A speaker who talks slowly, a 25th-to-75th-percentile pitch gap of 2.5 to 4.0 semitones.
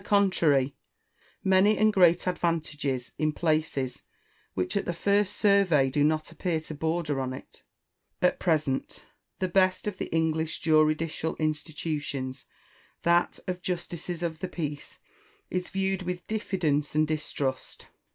Yes: slow, 130 wpm; average, 3.4 semitones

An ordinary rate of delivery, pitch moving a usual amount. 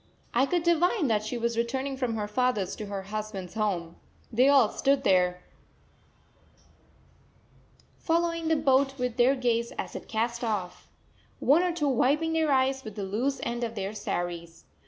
Yes: average, 165 wpm; average, 4.8 semitones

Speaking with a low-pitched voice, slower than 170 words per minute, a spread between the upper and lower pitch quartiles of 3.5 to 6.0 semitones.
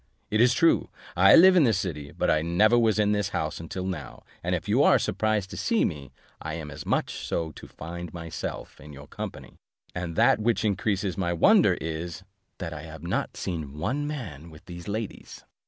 No: very low, 90 Hz; fast, 205 wpm; average, 5.1 semitones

